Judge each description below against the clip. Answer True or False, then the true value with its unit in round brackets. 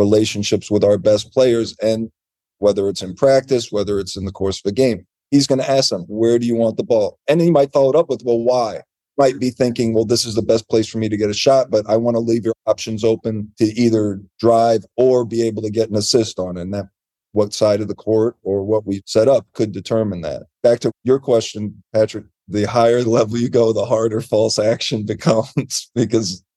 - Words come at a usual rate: False (235 wpm)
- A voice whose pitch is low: True (110 Hz)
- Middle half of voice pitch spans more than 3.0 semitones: False (2.5 semitones)